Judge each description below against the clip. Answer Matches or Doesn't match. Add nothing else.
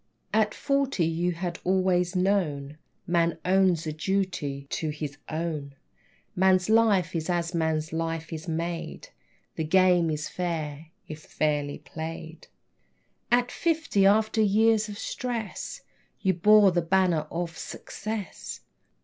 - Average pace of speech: Doesn't match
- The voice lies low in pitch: Doesn't match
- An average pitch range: Matches